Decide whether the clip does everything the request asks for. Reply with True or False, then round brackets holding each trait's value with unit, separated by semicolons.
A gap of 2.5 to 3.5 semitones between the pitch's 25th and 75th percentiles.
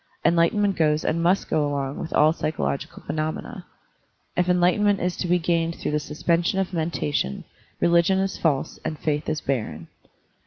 True (3.0 semitones)